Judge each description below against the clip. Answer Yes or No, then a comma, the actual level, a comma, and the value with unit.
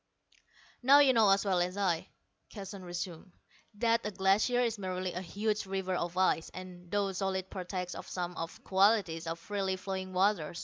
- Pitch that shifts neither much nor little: No, narrow, 2.1 semitones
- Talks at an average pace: Yes, average, 180 wpm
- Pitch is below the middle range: No, high, 190 Hz